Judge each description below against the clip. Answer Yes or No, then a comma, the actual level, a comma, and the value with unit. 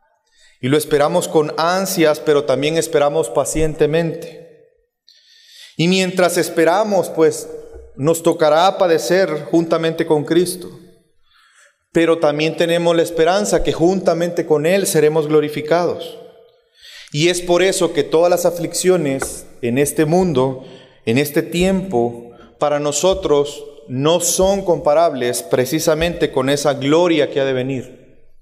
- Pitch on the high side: No, medium, 165 Hz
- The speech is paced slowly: Yes, slow, 120 wpm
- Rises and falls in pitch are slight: No, average, 3.5 semitones